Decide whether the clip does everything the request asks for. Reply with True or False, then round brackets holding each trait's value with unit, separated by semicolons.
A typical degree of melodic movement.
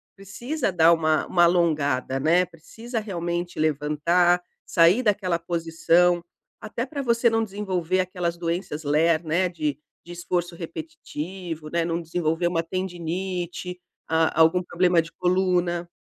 False (2.1 semitones)